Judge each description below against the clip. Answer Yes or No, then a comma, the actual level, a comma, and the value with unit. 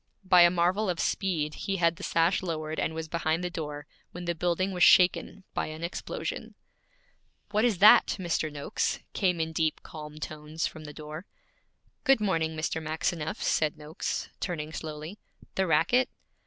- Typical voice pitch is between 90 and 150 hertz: No, medium, 165 Hz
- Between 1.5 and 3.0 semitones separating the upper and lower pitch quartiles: Yes, narrow, 2.6 semitones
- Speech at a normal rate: Yes, average, 170 wpm